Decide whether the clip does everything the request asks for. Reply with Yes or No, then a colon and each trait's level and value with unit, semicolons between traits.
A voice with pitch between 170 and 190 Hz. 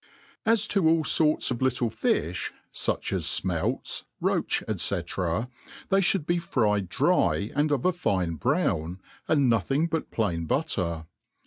No: low, 125 Hz